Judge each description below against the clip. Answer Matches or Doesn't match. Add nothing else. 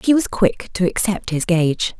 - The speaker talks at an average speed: Doesn't match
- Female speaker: Matches